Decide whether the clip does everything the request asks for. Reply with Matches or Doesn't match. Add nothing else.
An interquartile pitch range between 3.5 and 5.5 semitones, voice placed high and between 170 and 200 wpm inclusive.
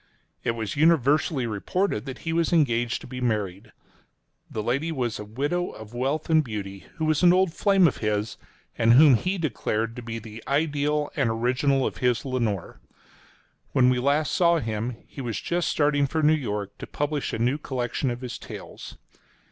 Doesn't match